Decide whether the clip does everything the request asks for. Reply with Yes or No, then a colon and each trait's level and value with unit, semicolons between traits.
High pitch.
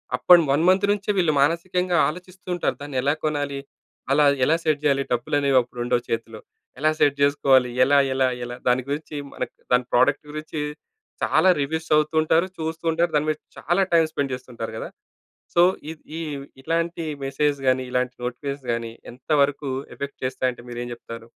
No: medium, 145 Hz